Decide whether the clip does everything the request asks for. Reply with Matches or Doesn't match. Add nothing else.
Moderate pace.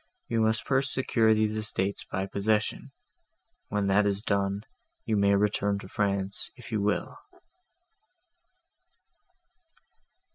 Doesn't match